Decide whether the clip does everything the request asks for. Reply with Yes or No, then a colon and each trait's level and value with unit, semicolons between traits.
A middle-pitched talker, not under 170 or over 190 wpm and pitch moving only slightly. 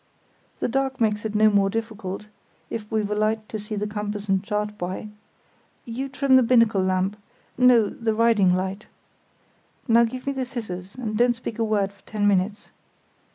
No: high, 215 Hz; average, 175 wpm; narrow, 2.3 semitones